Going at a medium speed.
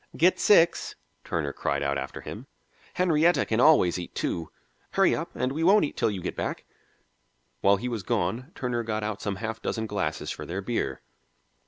Yes: average, 185 wpm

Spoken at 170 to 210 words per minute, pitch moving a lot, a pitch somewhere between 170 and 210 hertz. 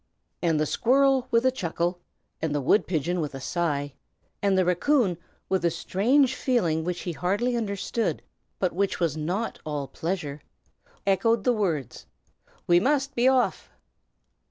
No: average, 155 wpm; wide, 6.3 semitones; medium, 185 Hz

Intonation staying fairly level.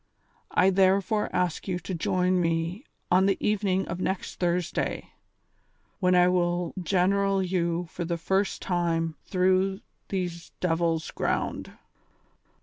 Yes: narrow, 1.9 semitones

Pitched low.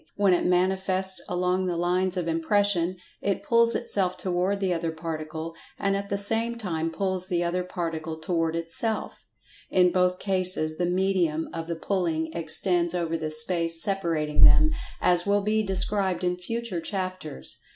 No: medium, 180 Hz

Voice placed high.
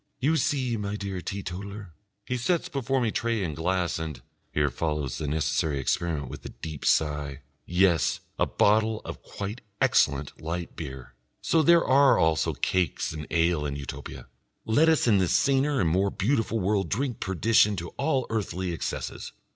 No: very low, 95 Hz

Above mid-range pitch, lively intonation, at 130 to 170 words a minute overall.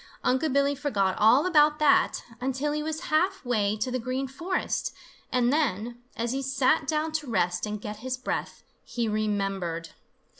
Yes: very high, 255 Hz; wide, 5.8 semitones; average, 165 wpm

